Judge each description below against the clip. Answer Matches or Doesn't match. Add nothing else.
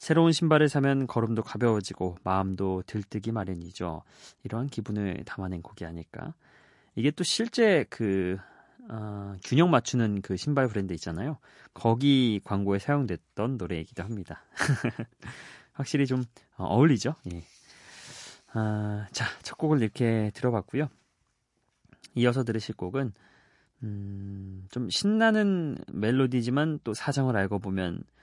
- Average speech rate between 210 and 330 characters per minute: Matches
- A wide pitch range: Matches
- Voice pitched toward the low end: Matches